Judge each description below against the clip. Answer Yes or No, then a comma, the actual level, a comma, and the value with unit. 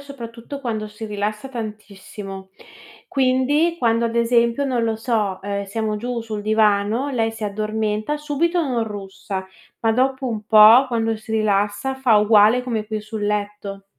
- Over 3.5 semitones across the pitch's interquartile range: No, average, 2.9 semitones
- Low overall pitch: No, high, 220 Hz